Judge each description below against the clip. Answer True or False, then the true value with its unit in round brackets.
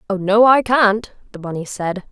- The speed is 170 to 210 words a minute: True (200 wpm)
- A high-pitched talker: True (205 Hz)